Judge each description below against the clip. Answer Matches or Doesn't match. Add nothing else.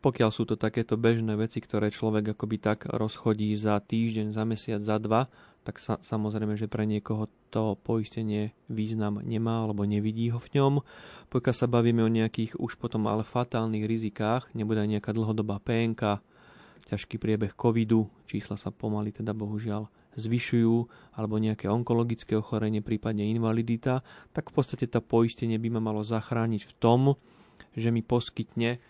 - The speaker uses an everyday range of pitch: Doesn't match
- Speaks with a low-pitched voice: Matches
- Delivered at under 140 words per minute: Doesn't match